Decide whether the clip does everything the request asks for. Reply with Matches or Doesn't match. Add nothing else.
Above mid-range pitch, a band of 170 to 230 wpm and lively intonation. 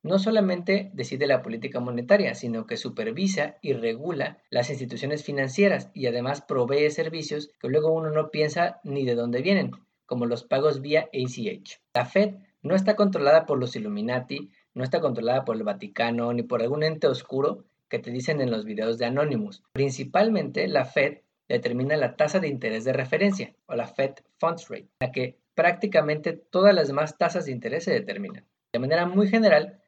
Doesn't match